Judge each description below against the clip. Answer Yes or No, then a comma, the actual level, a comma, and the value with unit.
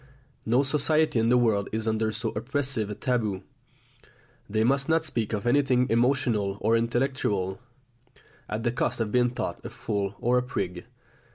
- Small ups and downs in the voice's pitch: No, average, 3.0 semitones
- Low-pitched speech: Yes, low, 115 Hz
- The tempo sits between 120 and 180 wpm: Yes, average, 165 wpm